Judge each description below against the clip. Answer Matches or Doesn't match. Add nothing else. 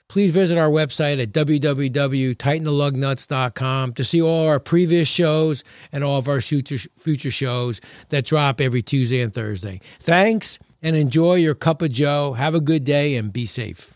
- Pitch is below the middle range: Doesn't match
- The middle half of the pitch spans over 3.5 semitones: Doesn't match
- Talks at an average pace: Matches